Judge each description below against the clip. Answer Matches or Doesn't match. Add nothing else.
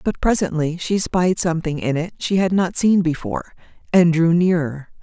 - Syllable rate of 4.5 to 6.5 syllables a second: Matches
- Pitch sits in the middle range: Matches